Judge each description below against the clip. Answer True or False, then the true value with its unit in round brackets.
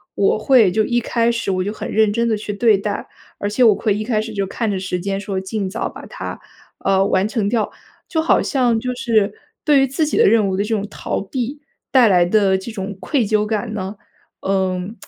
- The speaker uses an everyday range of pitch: True (3.0 semitones)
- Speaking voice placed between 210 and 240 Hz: True (215 Hz)